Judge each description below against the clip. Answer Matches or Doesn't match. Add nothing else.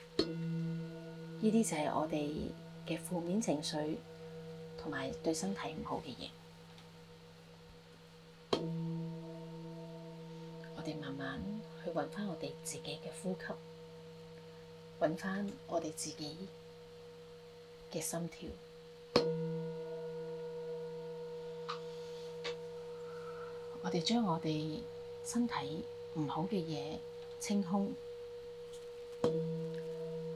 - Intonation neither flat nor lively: Matches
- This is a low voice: Doesn't match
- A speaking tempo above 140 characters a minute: Doesn't match